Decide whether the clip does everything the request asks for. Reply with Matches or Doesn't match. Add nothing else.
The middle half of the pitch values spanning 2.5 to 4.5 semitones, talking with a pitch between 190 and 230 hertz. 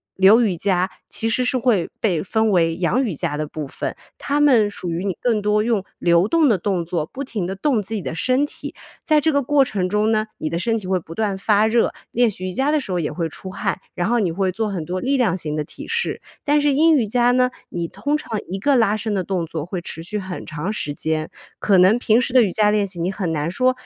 Doesn't match